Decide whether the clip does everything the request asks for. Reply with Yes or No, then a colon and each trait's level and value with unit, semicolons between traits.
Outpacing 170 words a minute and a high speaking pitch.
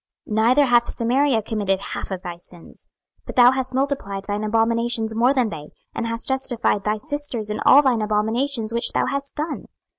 Yes: average, 185 wpm; high, 230 Hz